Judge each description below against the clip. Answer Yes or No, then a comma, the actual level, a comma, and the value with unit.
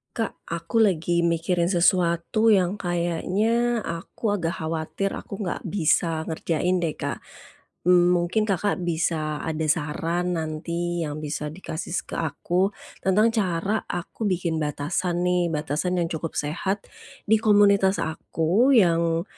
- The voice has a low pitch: No, medium, 175 Hz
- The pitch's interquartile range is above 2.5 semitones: Yes, average, 2.9 semitones